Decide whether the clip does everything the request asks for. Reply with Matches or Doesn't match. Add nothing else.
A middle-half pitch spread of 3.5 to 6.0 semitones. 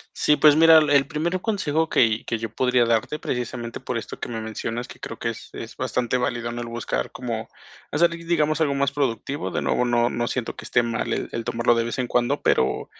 Matches